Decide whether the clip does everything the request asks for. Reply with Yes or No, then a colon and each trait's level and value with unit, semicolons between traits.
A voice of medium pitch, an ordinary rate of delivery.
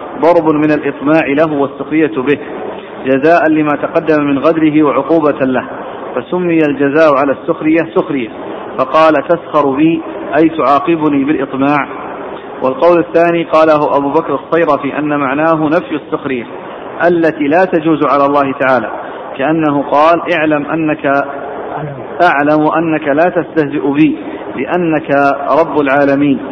Yes: medium, 150 Hz; average, 120 wpm